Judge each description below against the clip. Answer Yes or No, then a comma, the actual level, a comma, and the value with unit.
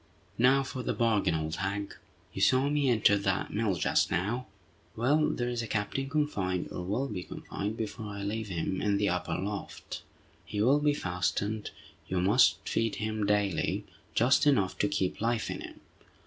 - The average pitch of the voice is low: Yes, low, 105 Hz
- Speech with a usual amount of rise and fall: Yes, average, 4.0 semitones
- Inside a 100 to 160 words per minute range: No, average, 175 wpm